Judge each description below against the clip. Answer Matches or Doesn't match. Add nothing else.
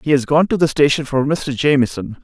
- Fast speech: Matches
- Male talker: Matches